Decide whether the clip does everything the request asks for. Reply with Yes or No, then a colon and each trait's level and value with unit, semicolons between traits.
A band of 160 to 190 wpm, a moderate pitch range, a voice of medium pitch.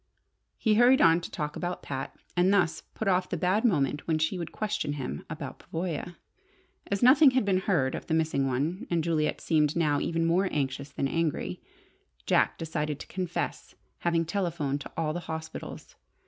Yes: average, 180 wpm; average, 3.5 semitones; medium, 165 Hz